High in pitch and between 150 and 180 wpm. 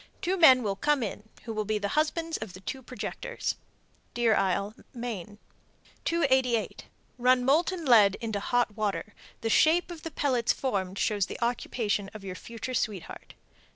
Yes: high, 235 Hz; average, 160 wpm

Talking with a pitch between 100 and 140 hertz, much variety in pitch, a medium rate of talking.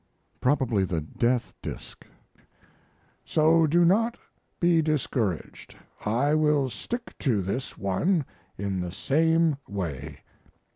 No: low, 135 Hz; wide, 8.7 semitones; slow, 105 wpm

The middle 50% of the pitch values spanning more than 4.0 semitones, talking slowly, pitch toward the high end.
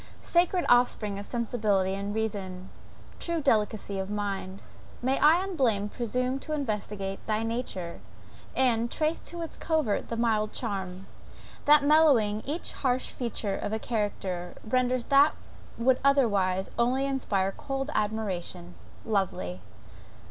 Yes: average, 5.1 semitones; slow, 125 wpm; high, 220 Hz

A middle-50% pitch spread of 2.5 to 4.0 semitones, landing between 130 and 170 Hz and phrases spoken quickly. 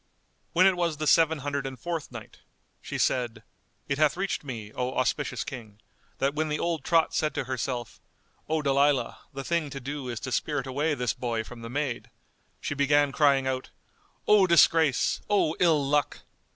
No: average, 3.4 semitones; medium, 140 Hz; average, 180 wpm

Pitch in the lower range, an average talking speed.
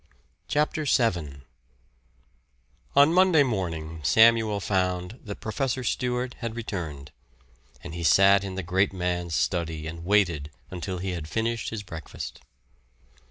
No: very low, 95 Hz; slow, 125 wpm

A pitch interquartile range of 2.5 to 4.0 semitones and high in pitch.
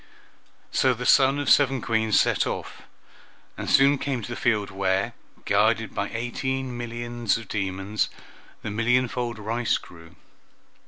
No: average, 3.2 semitones; low, 120 Hz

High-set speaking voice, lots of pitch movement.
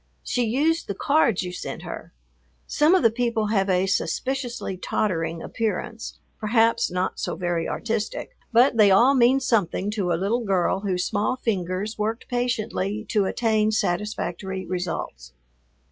No: high, 210 Hz; average, 4.1 semitones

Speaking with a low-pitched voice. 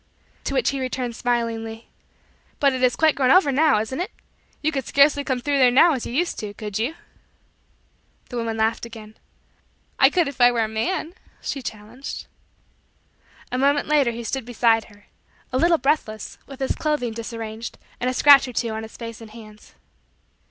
No: high, 245 Hz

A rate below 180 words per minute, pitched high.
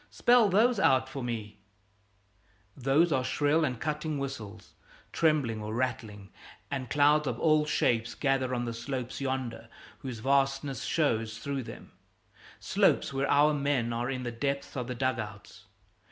No: average, 155 wpm; low, 130 Hz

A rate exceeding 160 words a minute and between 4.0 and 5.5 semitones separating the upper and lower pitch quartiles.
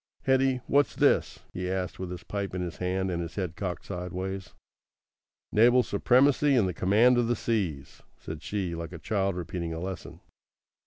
Yes: average, 175 wpm; average, 4.5 semitones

